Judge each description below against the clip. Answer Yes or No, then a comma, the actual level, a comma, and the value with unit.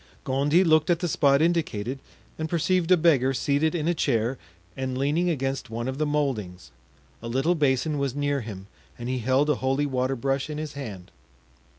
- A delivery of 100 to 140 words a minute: No, average, 190 wpm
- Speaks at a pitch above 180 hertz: No, medium, 140 Hz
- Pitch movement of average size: Yes, average, 3.2 semitones